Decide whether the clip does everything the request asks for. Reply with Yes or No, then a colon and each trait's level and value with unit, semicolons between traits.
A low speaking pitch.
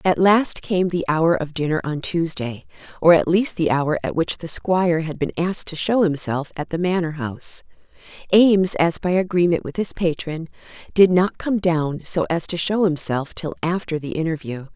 No: medium, 170 Hz